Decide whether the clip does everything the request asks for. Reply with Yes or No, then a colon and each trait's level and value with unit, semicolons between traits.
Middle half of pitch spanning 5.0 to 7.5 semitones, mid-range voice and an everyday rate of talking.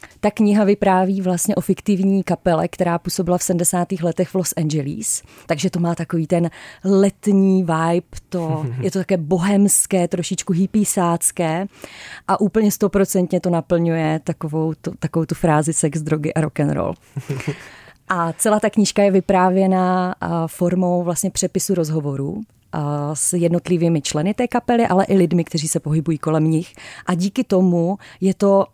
No: average, 2.8 semitones; medium, 180 Hz; average, 150 wpm